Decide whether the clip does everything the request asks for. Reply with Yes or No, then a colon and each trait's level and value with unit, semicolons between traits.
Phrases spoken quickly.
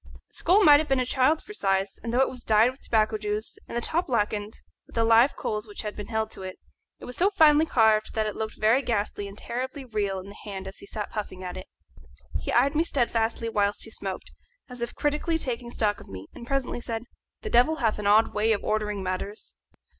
Yes: fast, 235 wpm